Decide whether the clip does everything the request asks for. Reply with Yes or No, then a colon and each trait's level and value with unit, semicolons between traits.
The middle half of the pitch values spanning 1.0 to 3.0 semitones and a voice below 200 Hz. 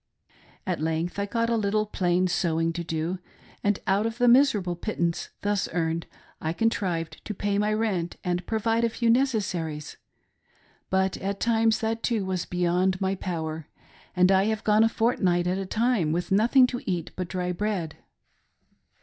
No: average, 4.0 semitones; high, 190 Hz